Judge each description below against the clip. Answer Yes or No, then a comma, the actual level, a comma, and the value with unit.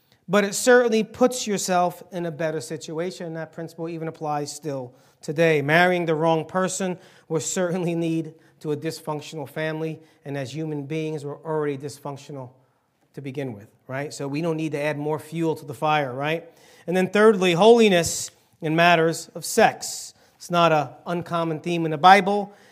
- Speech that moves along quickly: No, average, 170 wpm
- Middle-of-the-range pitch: Yes, medium, 160 Hz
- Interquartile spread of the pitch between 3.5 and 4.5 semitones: No, narrow, 2.5 semitones